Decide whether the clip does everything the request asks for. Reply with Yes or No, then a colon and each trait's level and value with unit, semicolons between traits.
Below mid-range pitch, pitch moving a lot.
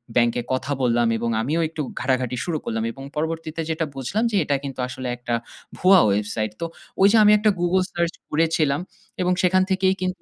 No: medium, 155 Hz; wide, 6.5 semitones